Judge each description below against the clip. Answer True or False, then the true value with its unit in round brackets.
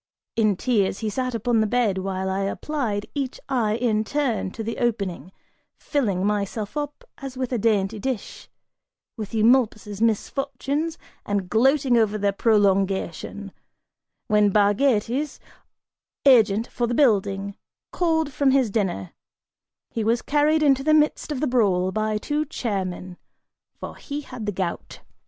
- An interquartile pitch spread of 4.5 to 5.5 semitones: True (4.8 semitones)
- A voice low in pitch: False (225 Hz)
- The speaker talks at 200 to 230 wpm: False (140 wpm)